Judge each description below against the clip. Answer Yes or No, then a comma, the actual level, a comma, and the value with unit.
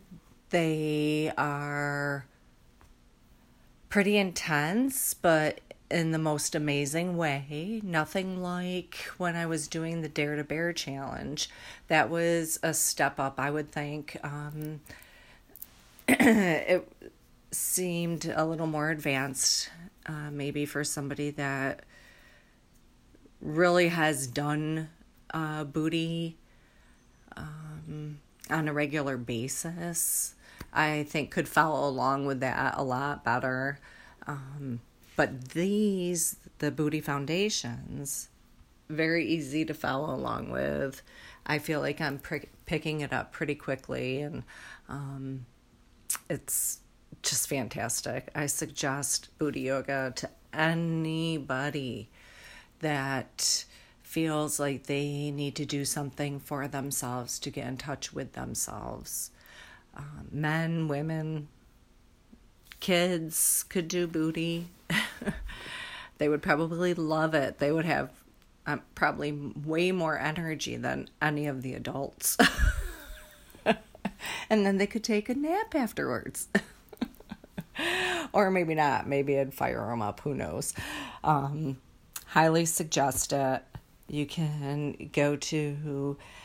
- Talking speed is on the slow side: Yes, slow, 110 wpm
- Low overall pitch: No, medium, 150 Hz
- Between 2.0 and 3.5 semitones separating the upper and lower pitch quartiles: Yes, average, 2.7 semitones